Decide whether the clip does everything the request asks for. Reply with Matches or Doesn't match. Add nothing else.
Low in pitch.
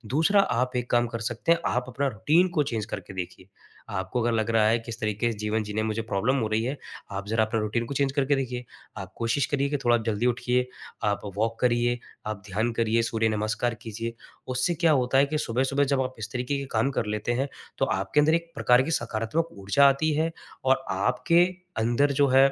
Matches